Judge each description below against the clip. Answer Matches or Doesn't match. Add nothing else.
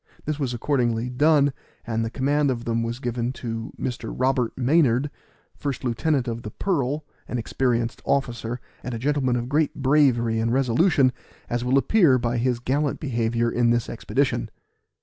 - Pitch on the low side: Matches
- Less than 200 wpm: Matches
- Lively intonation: Doesn't match